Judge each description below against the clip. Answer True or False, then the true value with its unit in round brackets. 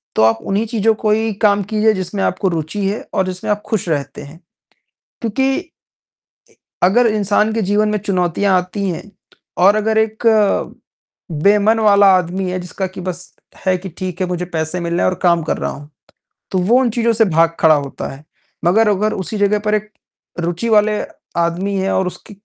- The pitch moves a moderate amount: True (3.1 semitones)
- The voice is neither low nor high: False (195 Hz)